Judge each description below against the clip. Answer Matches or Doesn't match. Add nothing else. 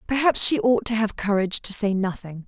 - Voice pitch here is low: Doesn't match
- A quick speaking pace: Matches